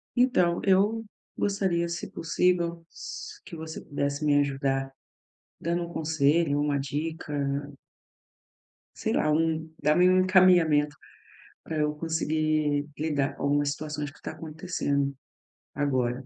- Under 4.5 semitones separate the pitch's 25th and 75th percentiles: Yes, average, 3.0 semitones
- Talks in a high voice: No, medium, 155 Hz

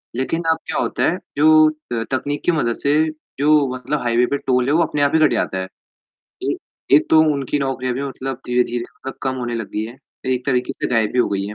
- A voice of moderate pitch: No, low, 130 Hz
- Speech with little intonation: No, average, 3.1 semitones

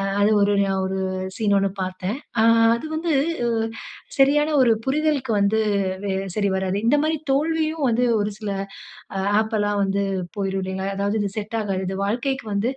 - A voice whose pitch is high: Yes, high, 210 Hz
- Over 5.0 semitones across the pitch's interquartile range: Yes, wide, 5.4 semitones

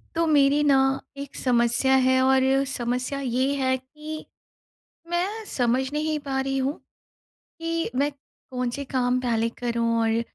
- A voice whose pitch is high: Yes, very high, 265 Hz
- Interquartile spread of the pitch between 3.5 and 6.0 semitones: No, narrow, 2.4 semitones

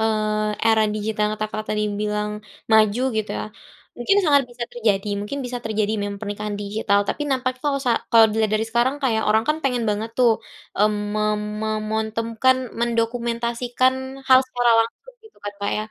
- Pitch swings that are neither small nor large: No, narrow, 2.3 semitones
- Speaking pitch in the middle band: No, high, 220 Hz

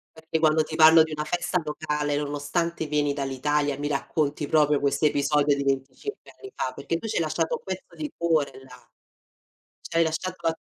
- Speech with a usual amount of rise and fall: No, narrow, 2.2 semitones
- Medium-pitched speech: Yes, medium, 150 Hz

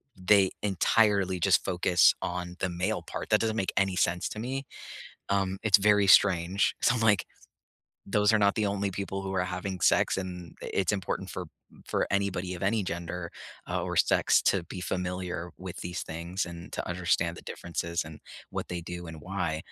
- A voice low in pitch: Yes, very low, 95 Hz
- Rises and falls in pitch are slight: Yes, narrow, 2.2 semitones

